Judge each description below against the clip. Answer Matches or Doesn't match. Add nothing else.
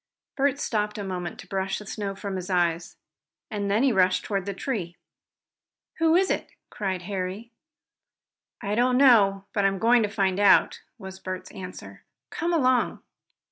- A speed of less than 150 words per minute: Doesn't match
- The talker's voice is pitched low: Doesn't match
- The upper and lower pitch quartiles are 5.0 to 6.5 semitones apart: Doesn't match